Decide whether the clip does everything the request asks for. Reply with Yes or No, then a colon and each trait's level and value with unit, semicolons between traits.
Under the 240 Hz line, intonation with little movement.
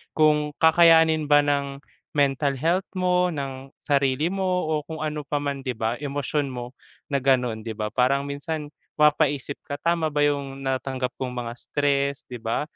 Yes: medium, 140 Hz; narrow, 2.3 semitones